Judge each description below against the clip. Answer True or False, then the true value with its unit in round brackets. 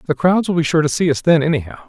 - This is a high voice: False (155 Hz)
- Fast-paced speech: True (320 wpm)